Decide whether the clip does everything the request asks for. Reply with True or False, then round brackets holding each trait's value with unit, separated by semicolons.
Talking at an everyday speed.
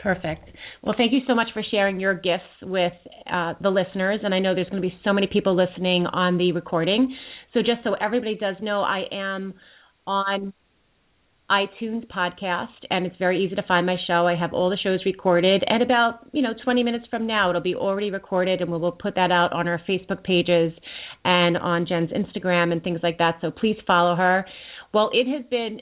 False (210 wpm)